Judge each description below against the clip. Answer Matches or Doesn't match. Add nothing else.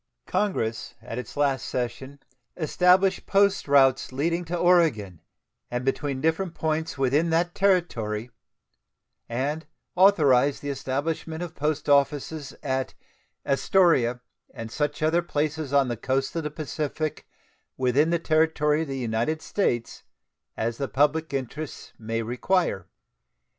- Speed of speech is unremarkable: Doesn't match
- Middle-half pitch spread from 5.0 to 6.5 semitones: Doesn't match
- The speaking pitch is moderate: Matches